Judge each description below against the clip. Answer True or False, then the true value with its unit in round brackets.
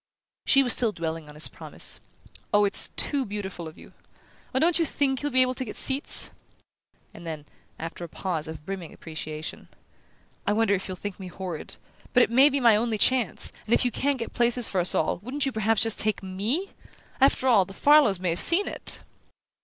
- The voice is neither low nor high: False (215 Hz)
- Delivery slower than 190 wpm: False (205 wpm)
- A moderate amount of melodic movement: False (6.2 semitones)